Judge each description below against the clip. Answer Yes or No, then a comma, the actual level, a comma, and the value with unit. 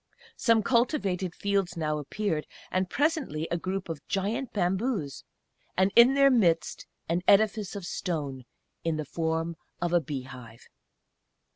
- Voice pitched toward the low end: No, medium, 180 Hz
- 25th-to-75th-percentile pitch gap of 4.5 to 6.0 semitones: Yes, average, 4.8 semitones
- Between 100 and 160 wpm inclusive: Yes, average, 140 wpm